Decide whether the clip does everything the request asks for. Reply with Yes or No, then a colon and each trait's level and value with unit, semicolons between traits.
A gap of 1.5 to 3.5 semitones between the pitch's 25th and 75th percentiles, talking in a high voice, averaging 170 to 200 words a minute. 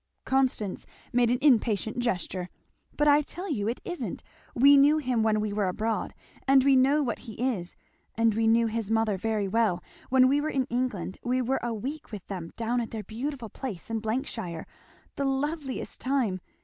No: average, 3.9 semitones; high, 235 Hz; average, 190 wpm